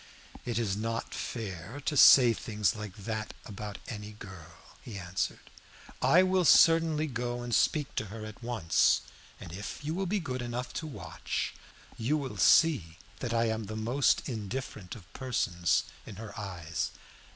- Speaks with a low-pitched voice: Yes, low, 115 Hz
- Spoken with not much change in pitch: No, average, 4.5 semitones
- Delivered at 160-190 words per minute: Yes, average, 165 wpm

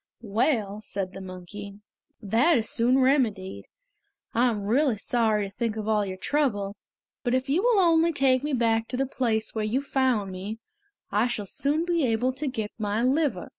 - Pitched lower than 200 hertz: No, high, 235 Hz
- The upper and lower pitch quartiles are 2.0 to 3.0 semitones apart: No, average, 4.5 semitones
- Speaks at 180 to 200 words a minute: Yes, average, 185 wpm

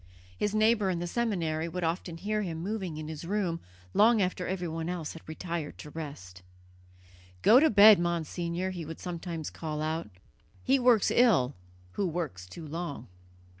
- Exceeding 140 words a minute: Yes, average, 165 wpm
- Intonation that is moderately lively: Yes, average, 3.9 semitones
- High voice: No, medium, 170 Hz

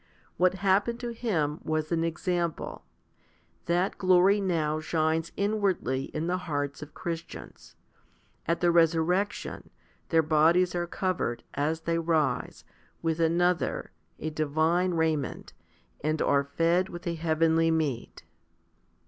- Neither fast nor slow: No, slow, 125 wpm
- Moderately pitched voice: Yes, medium, 165 Hz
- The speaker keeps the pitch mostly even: Yes, narrow, 2.3 semitones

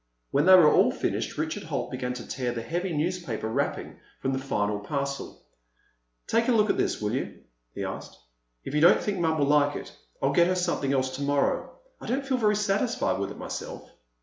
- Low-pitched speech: No, medium, 145 Hz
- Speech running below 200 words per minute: No, fast, 205 wpm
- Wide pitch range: Yes, wide, 6.0 semitones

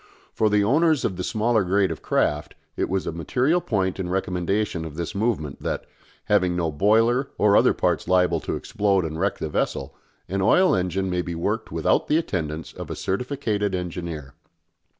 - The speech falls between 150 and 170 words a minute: No, average, 185 wpm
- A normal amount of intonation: Yes, average, 3.8 semitones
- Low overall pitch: Yes, very low, 95 Hz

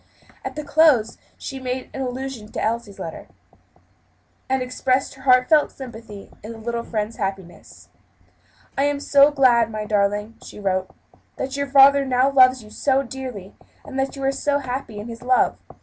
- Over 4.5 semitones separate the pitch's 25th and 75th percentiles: No, average, 3.8 semitones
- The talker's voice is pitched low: No, very high, 255 Hz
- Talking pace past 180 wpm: No, average, 170 wpm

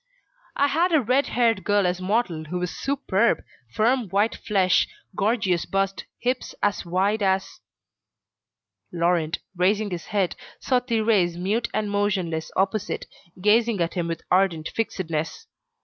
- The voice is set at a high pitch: Yes, high, 195 Hz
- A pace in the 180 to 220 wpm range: No, average, 140 wpm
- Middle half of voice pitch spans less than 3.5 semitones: No, average, 4.1 semitones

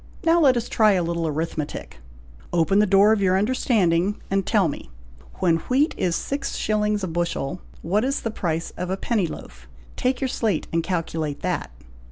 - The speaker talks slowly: No, average, 185 wpm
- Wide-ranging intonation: No, average, 4.7 semitones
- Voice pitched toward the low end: No, high, 190 Hz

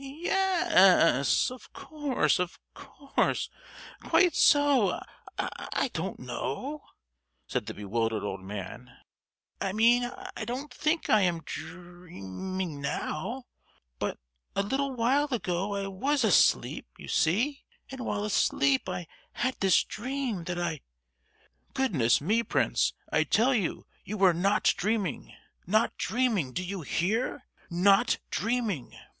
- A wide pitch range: Yes, wide, 6.7 semitones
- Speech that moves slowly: Yes, slow, 120 wpm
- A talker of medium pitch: No, high, 200 Hz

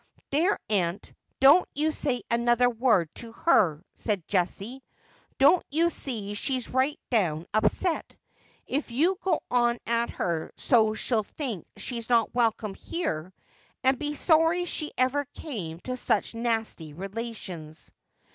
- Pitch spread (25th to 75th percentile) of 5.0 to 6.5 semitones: Yes, wide, 5.6 semitones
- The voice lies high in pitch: Yes, high, 235 Hz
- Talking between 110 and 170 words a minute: Yes, average, 140 wpm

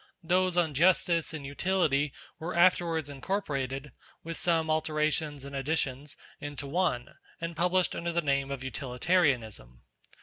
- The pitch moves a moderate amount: Yes, average, 3.8 semitones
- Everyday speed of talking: No, slow, 130 wpm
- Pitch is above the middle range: No, medium, 155 Hz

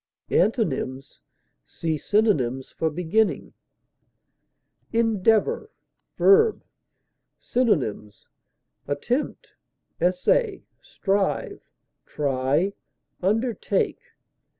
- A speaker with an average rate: No, slow, 55 wpm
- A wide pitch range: Yes, wide, 7.9 semitones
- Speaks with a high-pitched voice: Yes, high, 195 Hz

